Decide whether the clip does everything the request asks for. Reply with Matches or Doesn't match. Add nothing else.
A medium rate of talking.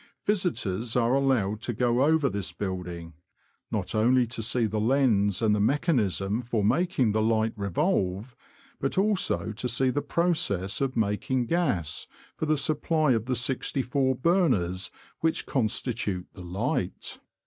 Matches